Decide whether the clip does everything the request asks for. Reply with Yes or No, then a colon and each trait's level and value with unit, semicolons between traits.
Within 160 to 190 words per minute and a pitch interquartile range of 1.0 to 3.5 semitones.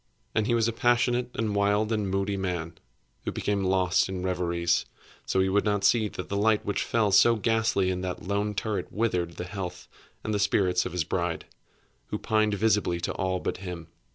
No: fast, 205 wpm; average, 2.9 semitones